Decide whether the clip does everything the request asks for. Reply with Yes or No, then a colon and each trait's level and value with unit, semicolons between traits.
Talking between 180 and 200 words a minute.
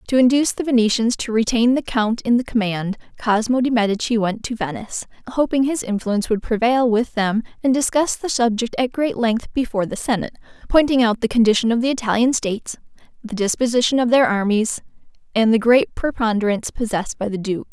Yes: average, 185 wpm